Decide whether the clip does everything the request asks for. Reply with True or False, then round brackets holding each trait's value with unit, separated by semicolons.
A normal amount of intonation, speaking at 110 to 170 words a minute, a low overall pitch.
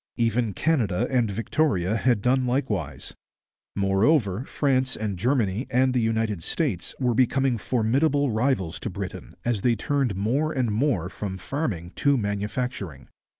True (4.7 semitones; 140 wpm; 115 Hz)